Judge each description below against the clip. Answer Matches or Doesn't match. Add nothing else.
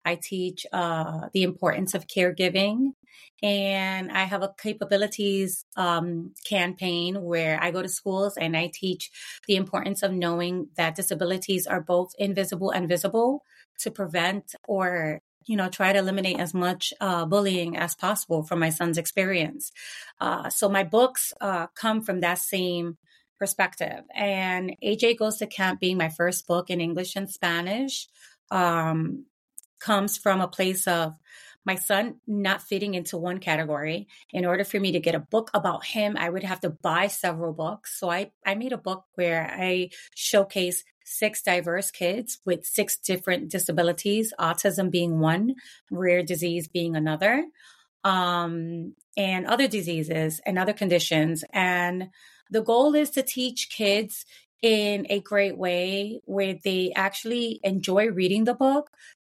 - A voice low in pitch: Doesn't match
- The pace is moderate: Matches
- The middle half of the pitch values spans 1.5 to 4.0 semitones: Matches